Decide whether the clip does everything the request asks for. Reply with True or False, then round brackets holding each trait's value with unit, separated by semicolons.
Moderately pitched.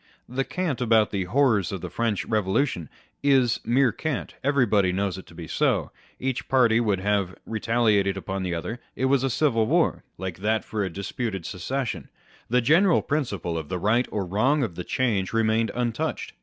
False (110 Hz)